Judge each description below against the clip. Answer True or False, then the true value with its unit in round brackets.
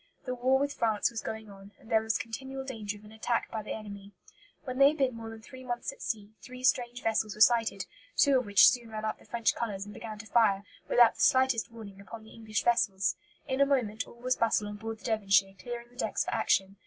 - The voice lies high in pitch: True (225 Hz)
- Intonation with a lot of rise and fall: False (2.7 semitones)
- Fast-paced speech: True (245 wpm)